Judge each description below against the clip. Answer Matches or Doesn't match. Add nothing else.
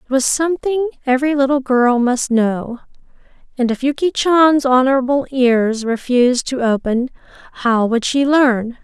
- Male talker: Doesn't match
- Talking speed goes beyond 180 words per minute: Doesn't match